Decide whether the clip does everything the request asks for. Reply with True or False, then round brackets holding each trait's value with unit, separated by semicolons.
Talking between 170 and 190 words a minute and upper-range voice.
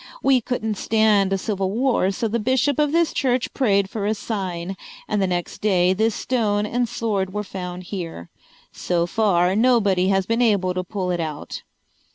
True (185 wpm; 205 Hz)